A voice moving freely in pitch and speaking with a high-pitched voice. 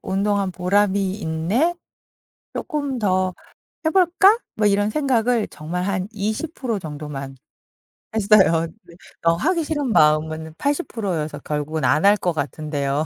Yes: wide, 6.6 semitones; high, 195 Hz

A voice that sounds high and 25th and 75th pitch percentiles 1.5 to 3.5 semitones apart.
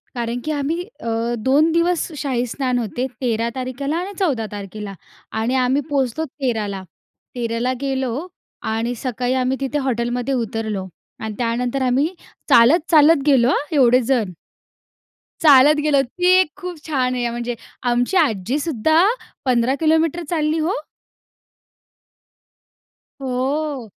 No: very high, 255 Hz; average, 4.1 semitones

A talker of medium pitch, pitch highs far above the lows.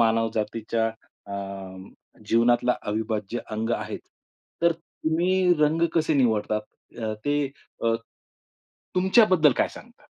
No: low, 120 Hz; wide, 6.5 semitones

